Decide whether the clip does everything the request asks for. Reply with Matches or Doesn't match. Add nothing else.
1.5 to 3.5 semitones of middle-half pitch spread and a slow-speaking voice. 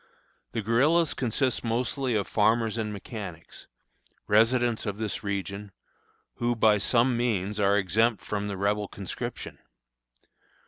Matches